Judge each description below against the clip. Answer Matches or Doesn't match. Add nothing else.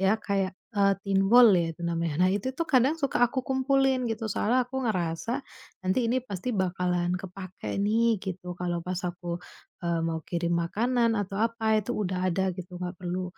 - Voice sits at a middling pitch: Doesn't match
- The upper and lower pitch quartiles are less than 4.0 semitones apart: Doesn't match